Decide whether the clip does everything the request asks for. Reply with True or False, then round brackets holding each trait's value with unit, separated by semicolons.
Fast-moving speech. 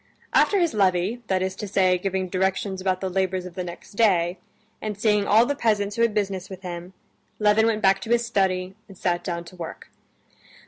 True (210 wpm)